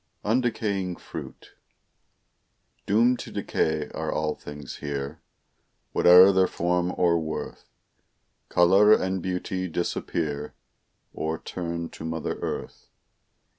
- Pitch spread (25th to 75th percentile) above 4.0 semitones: No, average, 3.2 semitones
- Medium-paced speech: No, slow, 100 wpm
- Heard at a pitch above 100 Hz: No, very low, 90 Hz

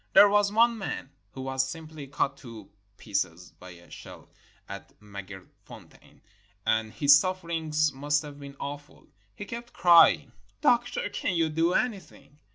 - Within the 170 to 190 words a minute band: No, average, 145 wpm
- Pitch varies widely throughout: Yes, wide, 5.8 semitones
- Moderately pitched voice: Yes, medium, 145 Hz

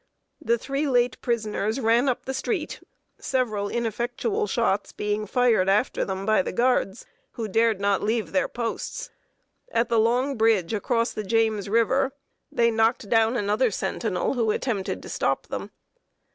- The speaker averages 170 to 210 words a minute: No, average, 155 wpm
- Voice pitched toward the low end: No, high, 230 Hz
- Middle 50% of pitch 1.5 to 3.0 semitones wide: Yes, average, 2.7 semitones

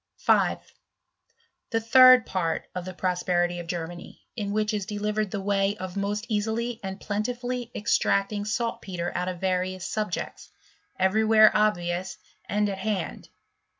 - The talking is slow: No, average, 150 wpm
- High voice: Yes, high, 205 Hz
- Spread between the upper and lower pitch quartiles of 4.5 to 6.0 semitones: No, average, 2.7 semitones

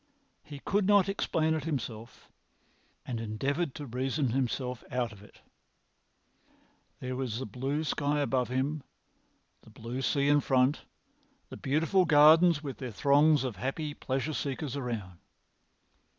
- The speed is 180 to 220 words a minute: No, slow, 135 wpm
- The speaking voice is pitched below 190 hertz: Yes, low, 135 Hz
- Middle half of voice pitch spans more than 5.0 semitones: No, average, 3.3 semitones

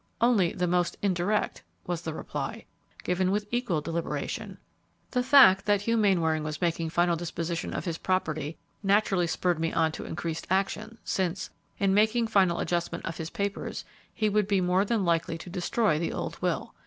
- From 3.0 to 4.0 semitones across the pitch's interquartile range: Yes, average, 3.5 semitones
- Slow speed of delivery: No, average, 175 wpm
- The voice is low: No, medium, 180 Hz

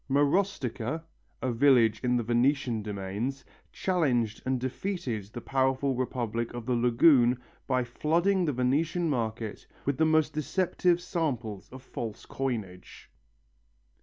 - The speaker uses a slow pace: Yes, slow, 125 wpm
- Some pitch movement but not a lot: Yes, average, 4.4 semitones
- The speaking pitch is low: Yes, low, 130 Hz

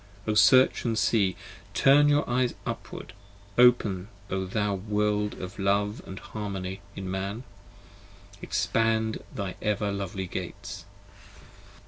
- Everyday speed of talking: No, slow, 115 wpm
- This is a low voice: Yes, low, 105 Hz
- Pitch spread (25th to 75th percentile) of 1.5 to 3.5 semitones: Yes, narrow, 2.6 semitones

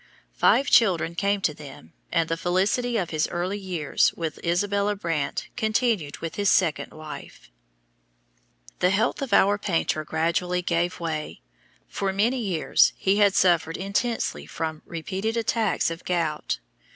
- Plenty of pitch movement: No, average, 3.8 semitones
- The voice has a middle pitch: Yes, medium, 180 Hz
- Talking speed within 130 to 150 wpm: Yes, average, 140 wpm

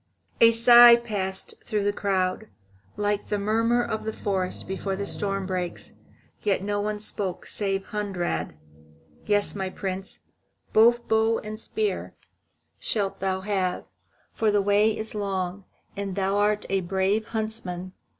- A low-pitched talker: No, high, 205 Hz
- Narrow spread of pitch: Yes, narrow, 2.2 semitones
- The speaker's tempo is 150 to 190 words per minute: No, average, 140 wpm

